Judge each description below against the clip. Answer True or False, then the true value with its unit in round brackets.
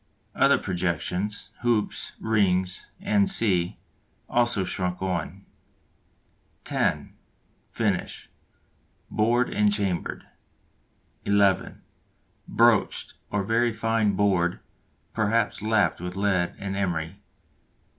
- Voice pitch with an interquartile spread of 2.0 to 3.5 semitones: True (3.2 semitones)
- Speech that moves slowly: True (85 wpm)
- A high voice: False (100 Hz)